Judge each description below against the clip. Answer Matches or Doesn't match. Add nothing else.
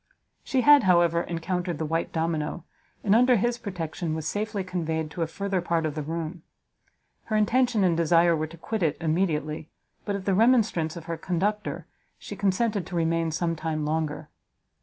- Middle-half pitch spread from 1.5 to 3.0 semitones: Doesn't match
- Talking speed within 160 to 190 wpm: Matches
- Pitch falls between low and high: Matches